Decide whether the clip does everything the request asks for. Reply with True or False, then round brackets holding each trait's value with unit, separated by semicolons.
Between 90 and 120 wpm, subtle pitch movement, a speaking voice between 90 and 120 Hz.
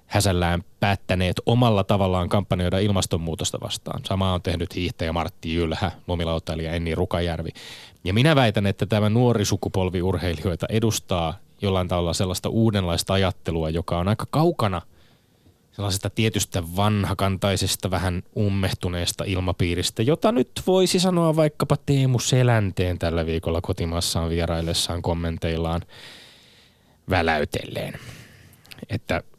False (110 wpm; 4.4 semitones; 95 Hz)